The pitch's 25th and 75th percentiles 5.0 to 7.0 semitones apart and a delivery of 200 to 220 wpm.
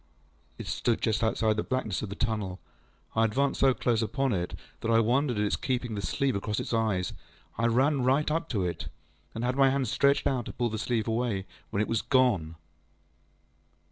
No: average, 3.4 semitones; fast, 205 wpm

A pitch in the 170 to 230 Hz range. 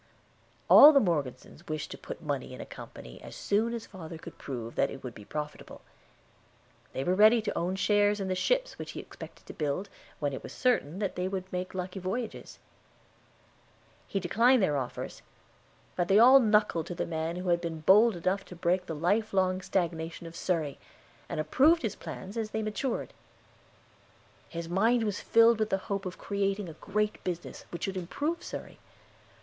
Yes: medium, 185 Hz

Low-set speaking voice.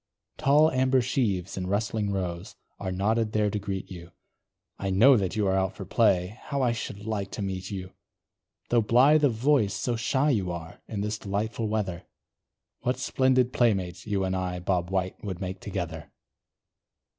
Yes: low, 100 Hz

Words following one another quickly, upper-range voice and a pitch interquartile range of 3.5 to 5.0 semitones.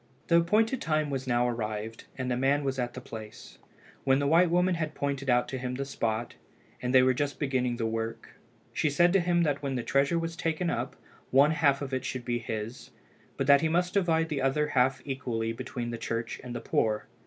No: fast, 220 wpm; low, 135 Hz; average, 4.1 semitones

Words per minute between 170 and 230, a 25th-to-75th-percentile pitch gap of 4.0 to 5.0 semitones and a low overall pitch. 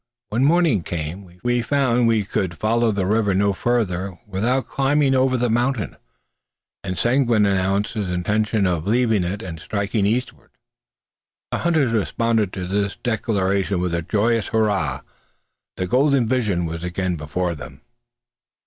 No: average, 145 wpm; average, 4.5 semitones; low, 105 Hz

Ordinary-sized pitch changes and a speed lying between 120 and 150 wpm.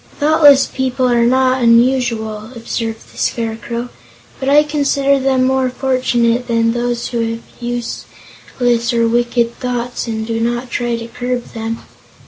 No: narrow, 1.8 semitones; average, 140 wpm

